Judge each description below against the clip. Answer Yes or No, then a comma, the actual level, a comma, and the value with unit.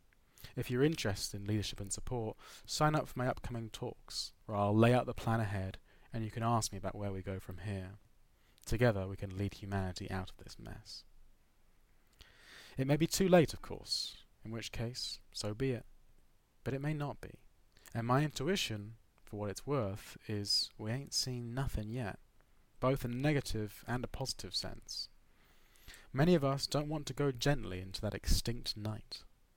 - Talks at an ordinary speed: Yes, average, 185 wpm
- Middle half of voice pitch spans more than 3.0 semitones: Yes, average, 4.2 semitones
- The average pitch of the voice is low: Yes, low, 115 Hz